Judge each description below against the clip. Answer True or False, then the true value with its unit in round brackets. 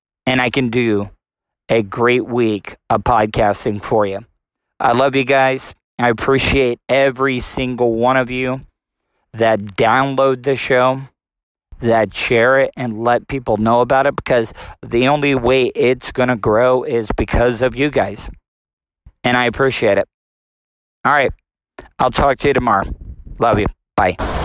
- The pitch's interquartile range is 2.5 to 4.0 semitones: True (3.2 semitones)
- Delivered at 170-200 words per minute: False (150 wpm)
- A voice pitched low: True (125 Hz)